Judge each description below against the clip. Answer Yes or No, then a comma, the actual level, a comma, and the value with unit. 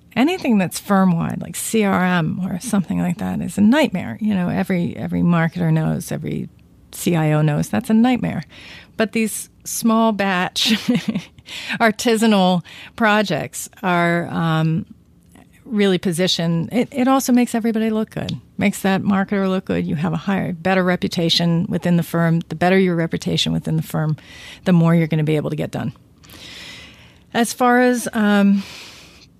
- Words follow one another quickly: No, average, 155 wpm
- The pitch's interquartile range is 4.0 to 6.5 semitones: Yes, average, 4.3 semitones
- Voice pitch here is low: No, high, 190 Hz